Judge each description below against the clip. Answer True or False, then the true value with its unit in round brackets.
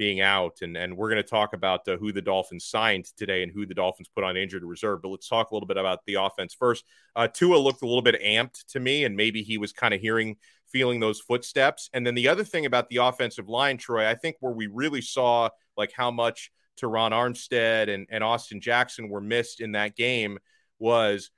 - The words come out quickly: True (235 wpm)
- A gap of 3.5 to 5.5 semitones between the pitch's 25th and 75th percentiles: False (3.0 semitones)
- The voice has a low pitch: True (115 Hz)